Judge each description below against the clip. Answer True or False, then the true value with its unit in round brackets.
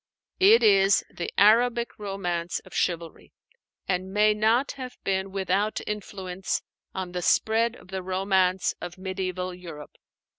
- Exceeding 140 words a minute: False (135 wpm)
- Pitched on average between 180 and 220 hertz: True (190 Hz)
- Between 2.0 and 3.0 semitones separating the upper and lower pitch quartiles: True (2.6 semitones)